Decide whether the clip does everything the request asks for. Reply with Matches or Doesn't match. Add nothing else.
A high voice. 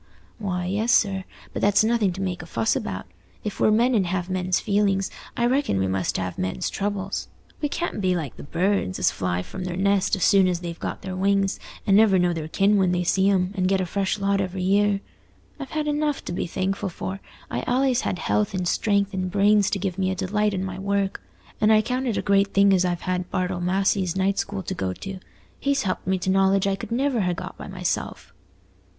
Matches